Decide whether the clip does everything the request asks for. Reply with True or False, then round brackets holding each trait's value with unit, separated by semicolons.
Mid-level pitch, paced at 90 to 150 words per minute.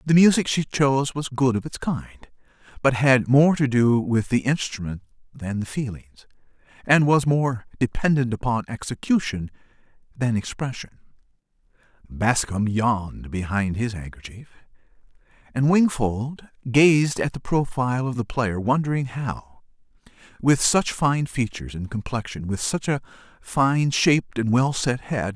False (125 Hz; 140 wpm)